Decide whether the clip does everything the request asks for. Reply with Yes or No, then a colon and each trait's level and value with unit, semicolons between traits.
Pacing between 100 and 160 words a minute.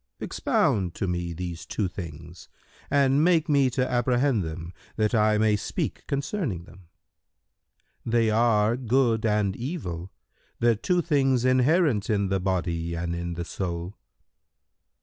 Yes: average, 140 wpm